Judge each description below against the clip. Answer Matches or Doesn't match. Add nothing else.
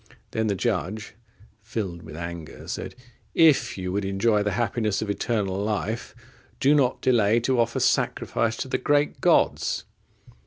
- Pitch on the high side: Doesn't match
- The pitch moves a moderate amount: Matches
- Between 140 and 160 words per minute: Matches